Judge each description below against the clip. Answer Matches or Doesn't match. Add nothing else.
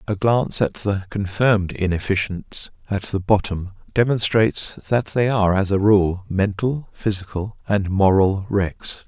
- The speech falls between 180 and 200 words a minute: Doesn't match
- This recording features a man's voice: Matches